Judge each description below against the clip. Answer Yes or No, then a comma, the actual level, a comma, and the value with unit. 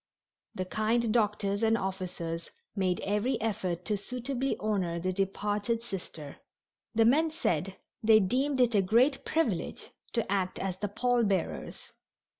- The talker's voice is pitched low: No, high, 210 Hz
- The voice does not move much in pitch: No, average, 4.0 semitones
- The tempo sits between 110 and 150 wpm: Yes, average, 140 wpm